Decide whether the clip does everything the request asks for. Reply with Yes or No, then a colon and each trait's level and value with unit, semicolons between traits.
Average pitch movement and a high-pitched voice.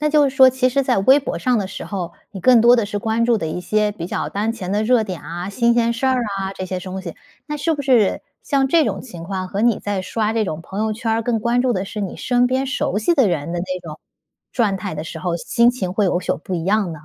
Yes: average, 4.7 semitones; high, 215 Hz